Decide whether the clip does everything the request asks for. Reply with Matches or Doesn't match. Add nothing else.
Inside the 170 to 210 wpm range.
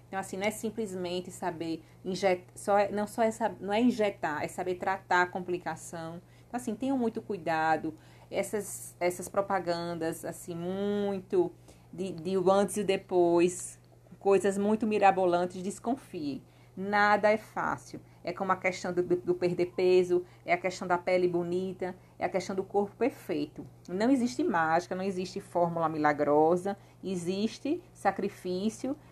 Doesn't match